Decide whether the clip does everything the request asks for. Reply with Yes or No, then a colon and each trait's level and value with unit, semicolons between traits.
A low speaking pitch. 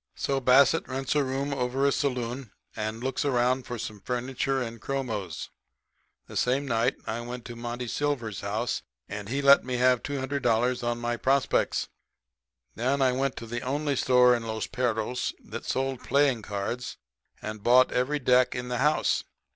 Yes: low, 125 Hz